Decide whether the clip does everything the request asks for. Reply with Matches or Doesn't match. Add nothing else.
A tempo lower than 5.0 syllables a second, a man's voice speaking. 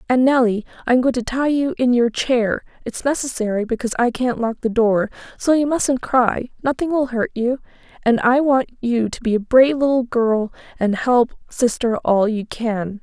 Doesn't match